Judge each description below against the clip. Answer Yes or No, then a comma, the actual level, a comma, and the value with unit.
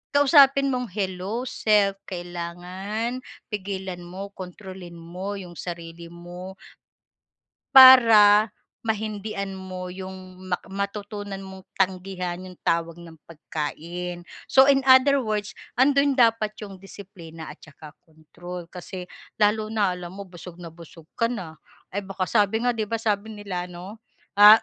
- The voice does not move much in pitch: No, average, 3.3 semitones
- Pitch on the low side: No, high, 190 Hz